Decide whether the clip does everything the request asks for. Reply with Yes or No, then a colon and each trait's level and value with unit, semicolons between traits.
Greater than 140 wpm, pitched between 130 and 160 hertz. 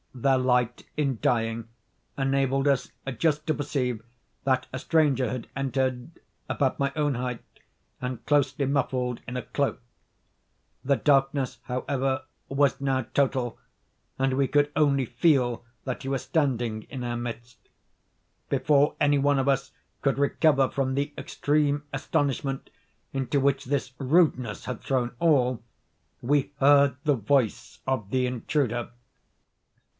No: slow, 135 wpm; low, 135 Hz